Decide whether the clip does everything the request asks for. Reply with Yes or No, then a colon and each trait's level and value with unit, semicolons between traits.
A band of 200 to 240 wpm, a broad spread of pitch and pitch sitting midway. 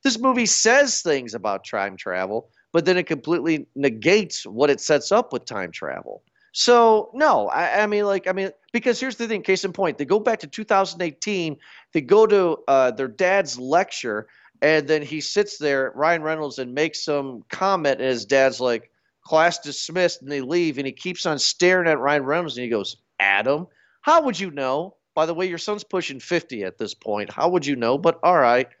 Yes: fast, 205 wpm; wide, 5.9 semitones; medium, 165 Hz